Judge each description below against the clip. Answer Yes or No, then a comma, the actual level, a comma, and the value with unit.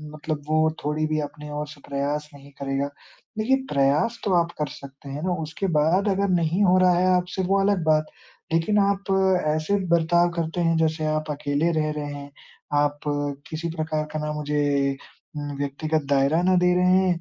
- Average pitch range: Yes, average, 3.5 semitones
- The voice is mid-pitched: Yes, medium, 155 Hz